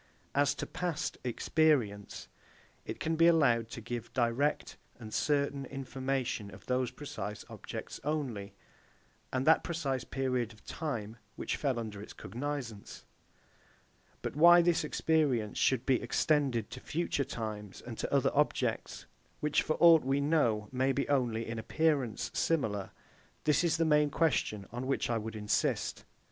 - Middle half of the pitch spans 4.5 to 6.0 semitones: Yes, average, 4.8 semitones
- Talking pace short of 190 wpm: Yes, average, 150 wpm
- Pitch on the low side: Yes, low, 130 Hz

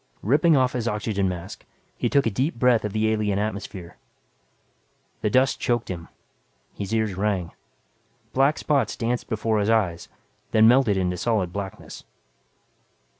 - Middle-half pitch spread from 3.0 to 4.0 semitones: Yes, average, 3.6 semitones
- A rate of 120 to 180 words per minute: Yes, average, 145 wpm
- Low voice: Yes, low, 110 Hz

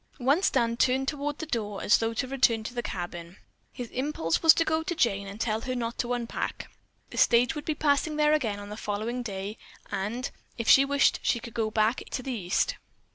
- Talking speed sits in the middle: No, fast, 220 wpm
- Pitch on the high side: Yes, high, 240 Hz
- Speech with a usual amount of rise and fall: Yes, average, 4.6 semitones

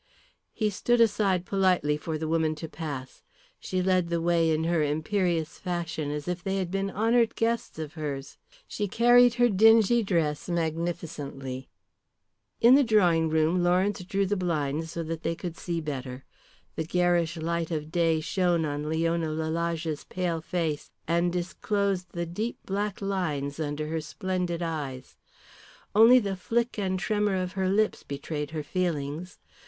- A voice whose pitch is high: No, medium, 170 Hz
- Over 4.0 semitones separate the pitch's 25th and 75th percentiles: No, average, 3.4 semitones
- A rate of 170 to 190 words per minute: No, average, 160 wpm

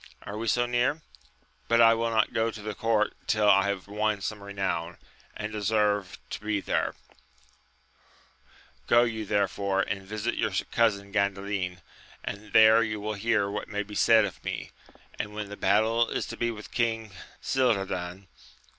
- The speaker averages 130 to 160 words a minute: No, average, 170 wpm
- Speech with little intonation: Yes, narrow, 2.1 semitones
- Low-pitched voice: Yes, low, 105 Hz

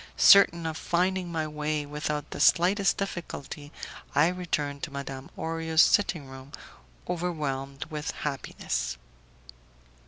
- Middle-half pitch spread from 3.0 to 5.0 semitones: Yes, average, 3.3 semitones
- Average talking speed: No, slow, 115 wpm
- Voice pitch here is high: No, medium, 155 Hz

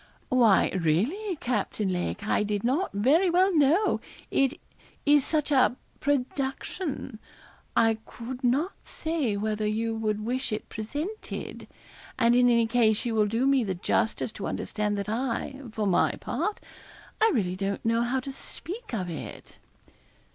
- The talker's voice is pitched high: Yes, high, 240 Hz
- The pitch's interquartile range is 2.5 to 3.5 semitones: No, average, 4.9 semitones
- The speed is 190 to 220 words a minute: No, average, 150 wpm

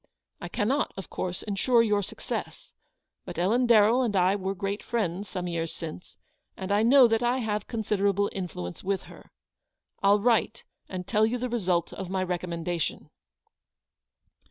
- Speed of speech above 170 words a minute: No, average, 155 wpm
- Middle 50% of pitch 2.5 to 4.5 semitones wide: Yes, average, 3.7 semitones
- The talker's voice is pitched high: Yes, high, 200 Hz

